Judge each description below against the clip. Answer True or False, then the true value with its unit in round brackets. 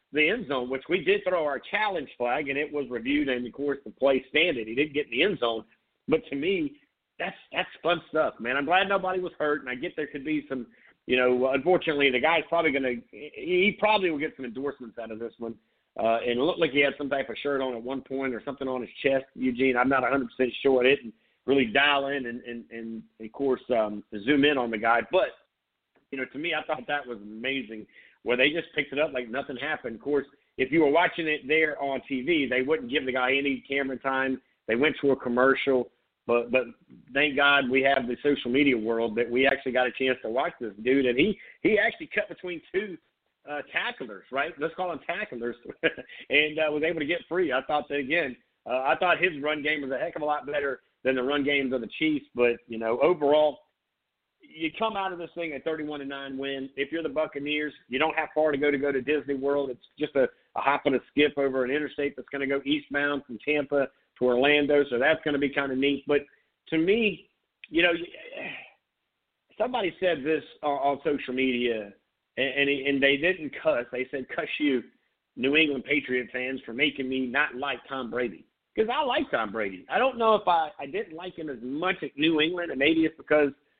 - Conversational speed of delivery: False (235 wpm)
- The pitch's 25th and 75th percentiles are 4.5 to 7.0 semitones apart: False (3.1 semitones)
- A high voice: False (140 Hz)